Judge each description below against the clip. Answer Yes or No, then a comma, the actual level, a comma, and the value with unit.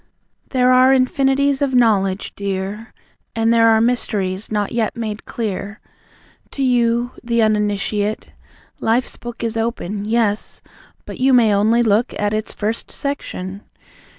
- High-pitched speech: Yes, high, 225 Hz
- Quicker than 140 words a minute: No, slow, 135 wpm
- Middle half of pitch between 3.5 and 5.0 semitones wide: No, average, 2.8 semitones